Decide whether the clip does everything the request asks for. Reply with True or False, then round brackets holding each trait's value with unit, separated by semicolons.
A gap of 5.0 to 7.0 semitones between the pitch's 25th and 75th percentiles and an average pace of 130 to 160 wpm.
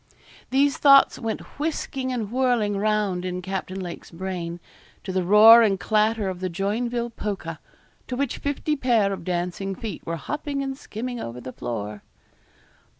True (5.3 semitones; 155 wpm)